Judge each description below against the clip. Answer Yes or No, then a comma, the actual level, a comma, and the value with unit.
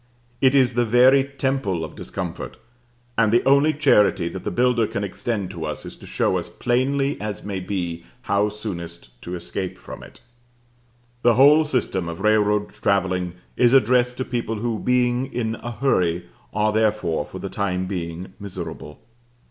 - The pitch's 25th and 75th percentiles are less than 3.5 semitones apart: No, average, 5.2 semitones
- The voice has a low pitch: Yes, low, 105 Hz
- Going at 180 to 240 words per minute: No, average, 165 wpm